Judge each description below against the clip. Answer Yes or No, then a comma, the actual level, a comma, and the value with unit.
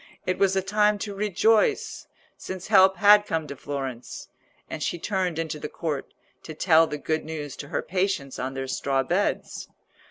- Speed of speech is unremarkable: Yes, average, 180 wpm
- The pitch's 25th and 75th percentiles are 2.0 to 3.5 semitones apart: No, average, 5.1 semitones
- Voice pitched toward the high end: No, medium, 165 Hz